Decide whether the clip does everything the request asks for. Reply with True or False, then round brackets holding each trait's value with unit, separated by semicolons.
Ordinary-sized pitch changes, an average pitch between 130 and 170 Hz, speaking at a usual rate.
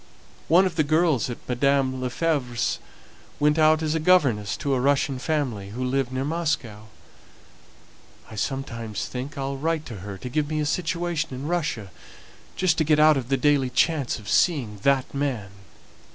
True (4.0 semitones; 140 Hz; 170 wpm)